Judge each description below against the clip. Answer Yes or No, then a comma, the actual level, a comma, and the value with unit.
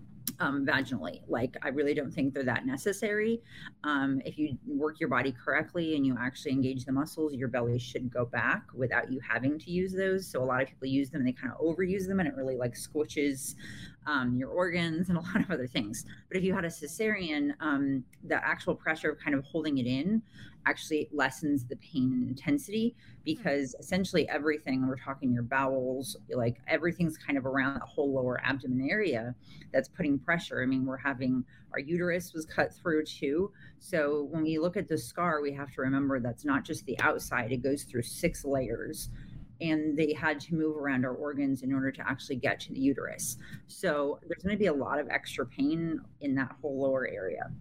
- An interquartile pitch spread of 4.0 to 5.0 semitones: No, average, 3.6 semitones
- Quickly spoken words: Yes, fast, 210 wpm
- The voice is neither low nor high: Yes, medium, 145 Hz